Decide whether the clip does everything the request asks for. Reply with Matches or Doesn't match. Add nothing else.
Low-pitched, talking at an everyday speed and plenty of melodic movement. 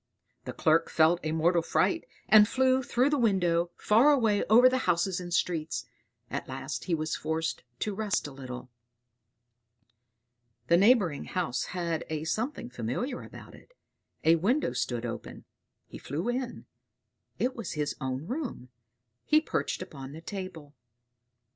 Doesn't match